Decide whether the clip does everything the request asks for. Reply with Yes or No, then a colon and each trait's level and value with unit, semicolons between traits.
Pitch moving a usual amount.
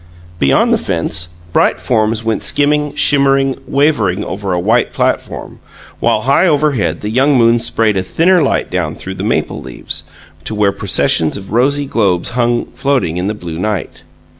No: wide, 6.1 semitones